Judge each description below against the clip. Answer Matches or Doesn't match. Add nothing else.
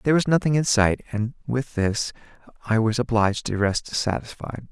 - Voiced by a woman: Doesn't match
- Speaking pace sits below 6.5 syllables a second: Matches